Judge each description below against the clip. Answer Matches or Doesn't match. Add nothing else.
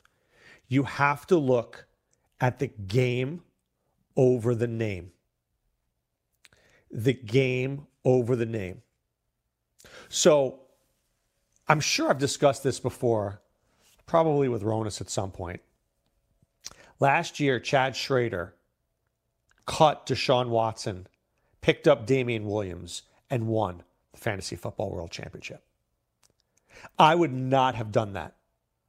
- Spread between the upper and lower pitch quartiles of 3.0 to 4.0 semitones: Doesn't match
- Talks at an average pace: Doesn't match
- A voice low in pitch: Matches